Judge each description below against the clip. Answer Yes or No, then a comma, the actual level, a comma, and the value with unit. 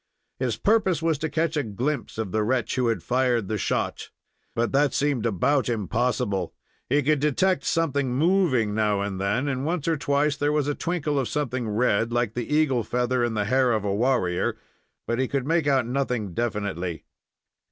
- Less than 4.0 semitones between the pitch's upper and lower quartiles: No, average, 4.8 semitones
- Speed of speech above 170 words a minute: Yes, average, 190 wpm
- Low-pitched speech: Yes, low, 125 Hz